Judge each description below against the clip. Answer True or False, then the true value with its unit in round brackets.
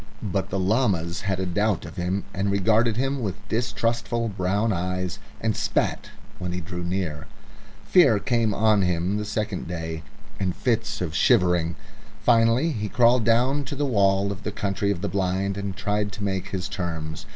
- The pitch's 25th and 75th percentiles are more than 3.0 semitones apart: True (3.6 semitones)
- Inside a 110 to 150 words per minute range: False (175 wpm)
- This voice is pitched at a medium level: False (100 Hz)